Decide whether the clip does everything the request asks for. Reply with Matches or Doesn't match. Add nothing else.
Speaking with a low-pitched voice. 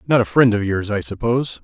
Matches